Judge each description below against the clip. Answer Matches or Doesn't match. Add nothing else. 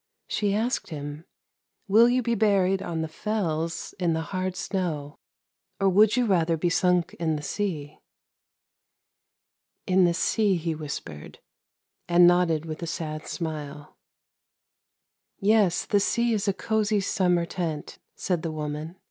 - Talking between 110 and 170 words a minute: Matches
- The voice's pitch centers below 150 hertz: Doesn't match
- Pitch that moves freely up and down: Doesn't match